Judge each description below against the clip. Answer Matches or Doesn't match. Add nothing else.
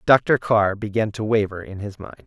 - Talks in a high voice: Doesn't match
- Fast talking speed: Matches